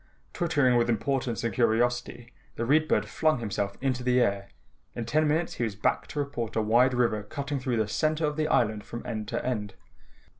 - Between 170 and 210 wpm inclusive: Yes, average, 200 wpm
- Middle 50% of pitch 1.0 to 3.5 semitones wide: No, average, 4.1 semitones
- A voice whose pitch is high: No, low, 120 Hz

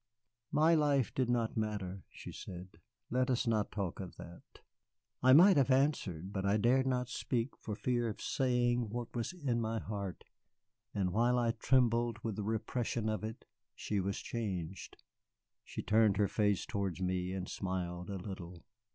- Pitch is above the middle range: No, low, 110 Hz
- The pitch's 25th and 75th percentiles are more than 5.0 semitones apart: No, average, 4.2 semitones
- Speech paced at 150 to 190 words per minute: Yes, average, 170 wpm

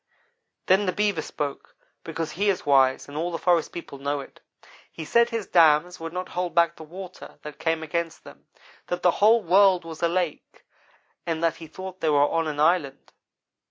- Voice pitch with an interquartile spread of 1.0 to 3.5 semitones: Yes, average, 2.9 semitones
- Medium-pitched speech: Yes, medium, 170 Hz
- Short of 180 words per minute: No, average, 195 wpm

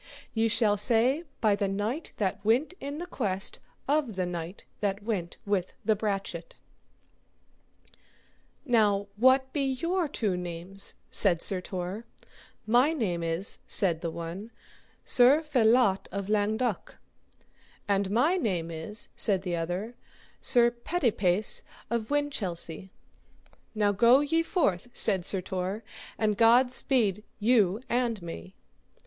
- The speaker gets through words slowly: Yes, slow, 130 wpm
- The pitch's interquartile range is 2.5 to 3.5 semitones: No, average, 4.7 semitones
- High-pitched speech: Yes, high, 210 Hz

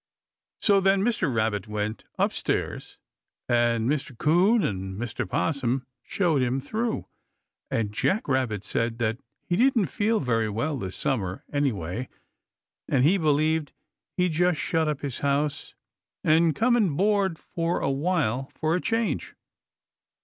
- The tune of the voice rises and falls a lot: Yes, wide, 7.4 semitones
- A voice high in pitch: No, medium, 145 Hz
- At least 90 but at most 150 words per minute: Yes, average, 140 wpm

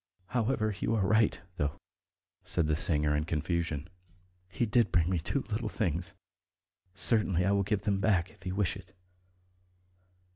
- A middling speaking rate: Yes, average, 155 wpm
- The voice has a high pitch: No, very low, 95 Hz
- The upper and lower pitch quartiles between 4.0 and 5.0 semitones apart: Yes, average, 4.3 semitones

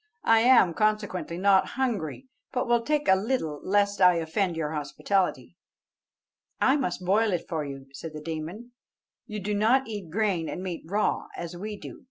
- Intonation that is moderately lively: Yes, average, 4.7 semitones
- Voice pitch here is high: Yes, high, 195 Hz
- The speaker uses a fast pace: No, average, 175 wpm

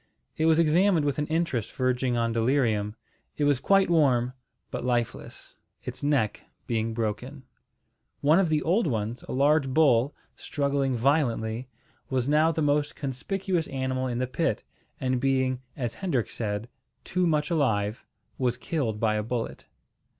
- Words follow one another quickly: No, average, 150 wpm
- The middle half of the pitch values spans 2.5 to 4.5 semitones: Yes, average, 4.2 semitones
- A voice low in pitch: Yes, low, 130 Hz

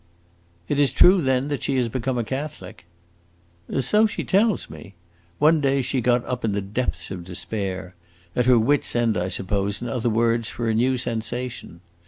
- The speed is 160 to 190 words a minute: Yes, average, 185 wpm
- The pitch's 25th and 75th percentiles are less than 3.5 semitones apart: No, average, 4.2 semitones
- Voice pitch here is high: No, low, 120 Hz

